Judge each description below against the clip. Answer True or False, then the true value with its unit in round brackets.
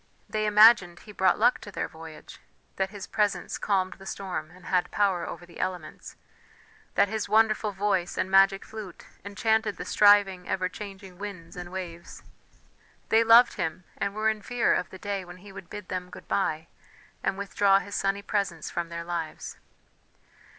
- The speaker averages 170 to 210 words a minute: True (175 wpm)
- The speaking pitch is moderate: False (195 Hz)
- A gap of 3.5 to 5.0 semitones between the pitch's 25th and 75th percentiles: False (2.5 semitones)